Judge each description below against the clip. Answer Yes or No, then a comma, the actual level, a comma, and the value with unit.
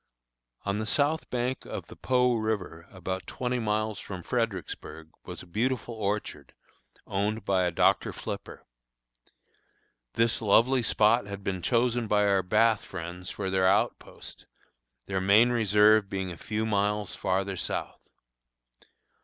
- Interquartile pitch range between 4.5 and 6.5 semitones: No, average, 3.2 semitones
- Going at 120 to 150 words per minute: Yes, slow, 135 wpm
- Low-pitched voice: Yes, low, 105 Hz